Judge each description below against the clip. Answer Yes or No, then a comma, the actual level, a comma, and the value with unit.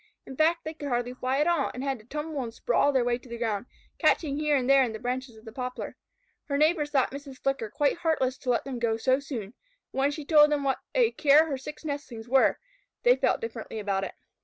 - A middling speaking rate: No, fast, 245 wpm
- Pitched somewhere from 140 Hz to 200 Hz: No, very high, 270 Hz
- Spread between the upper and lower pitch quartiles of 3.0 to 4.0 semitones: Yes, average, 3.5 semitones